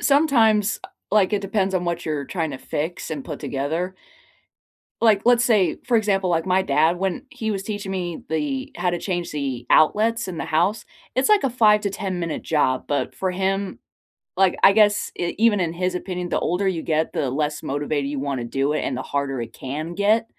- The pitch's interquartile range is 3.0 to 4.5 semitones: No, average, 5.2 semitones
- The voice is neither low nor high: Yes, medium, 180 Hz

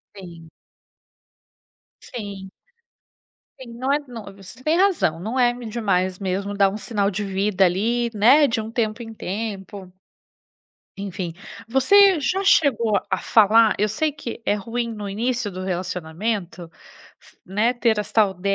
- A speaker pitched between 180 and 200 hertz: No, high, 215 Hz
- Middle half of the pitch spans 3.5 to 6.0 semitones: Yes, average, 3.8 semitones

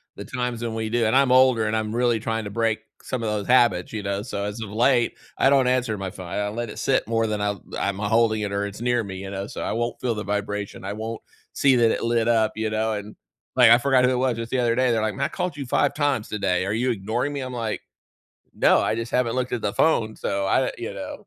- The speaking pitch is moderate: No, low, 115 Hz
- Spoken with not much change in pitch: No, average, 3.0 semitones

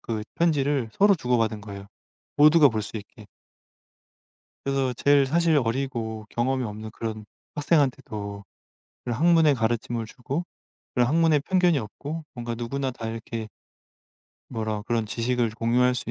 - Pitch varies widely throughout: No, average, 4.4 semitones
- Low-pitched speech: Yes, low, 120 Hz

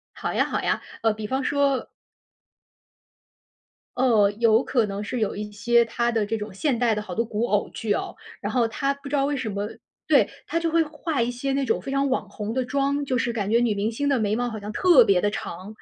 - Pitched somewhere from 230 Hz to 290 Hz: Yes, high, 235 Hz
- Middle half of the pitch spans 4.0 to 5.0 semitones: Yes, average, 4.5 semitones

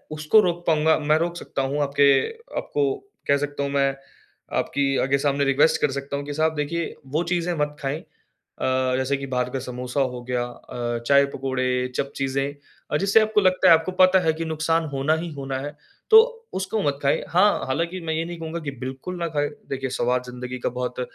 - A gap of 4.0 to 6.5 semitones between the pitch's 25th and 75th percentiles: No, average, 3.6 semitones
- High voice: No, medium, 145 Hz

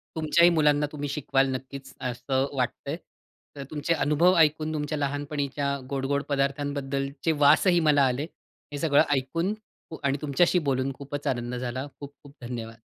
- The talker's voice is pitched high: No, medium, 140 Hz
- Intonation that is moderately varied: No, narrow, 1.9 semitones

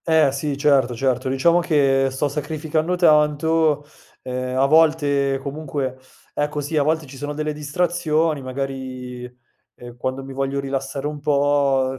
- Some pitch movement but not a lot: No, narrow, 2.3 semitones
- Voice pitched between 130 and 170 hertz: Yes, medium, 140 Hz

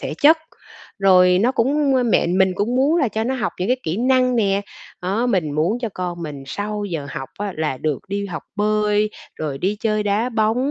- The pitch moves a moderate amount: Yes, average, 4.7 semitones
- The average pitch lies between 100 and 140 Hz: No, high, 205 Hz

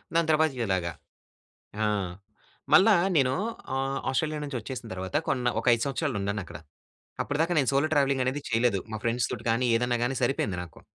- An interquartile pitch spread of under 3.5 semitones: No, average, 4.0 semitones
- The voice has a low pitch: Yes, low, 130 Hz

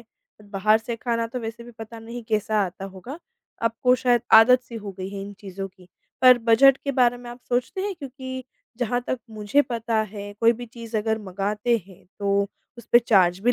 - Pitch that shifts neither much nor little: Yes, average, 3.1 semitones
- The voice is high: Yes, high, 230 Hz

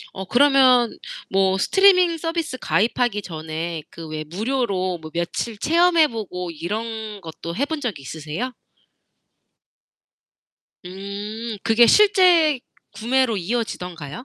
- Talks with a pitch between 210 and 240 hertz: Yes, high, 220 Hz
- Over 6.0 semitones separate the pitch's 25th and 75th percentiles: Yes, wide, 6.6 semitones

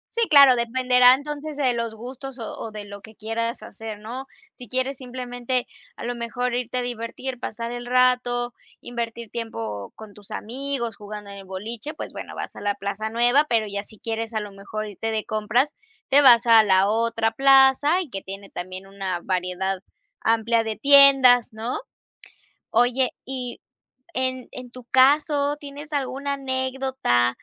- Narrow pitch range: No, average, 3.3 semitones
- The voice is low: No, high, 240 Hz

